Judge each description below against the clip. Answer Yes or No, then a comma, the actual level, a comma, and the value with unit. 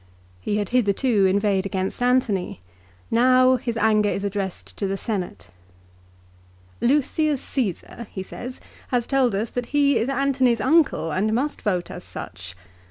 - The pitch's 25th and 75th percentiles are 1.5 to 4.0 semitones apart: No, average, 4.7 semitones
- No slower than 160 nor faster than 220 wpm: No, average, 145 wpm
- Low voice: No, high, 225 Hz